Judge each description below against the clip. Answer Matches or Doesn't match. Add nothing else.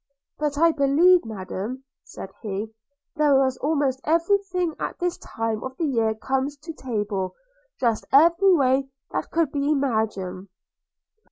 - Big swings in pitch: Matches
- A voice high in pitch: Matches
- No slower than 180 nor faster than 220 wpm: Doesn't match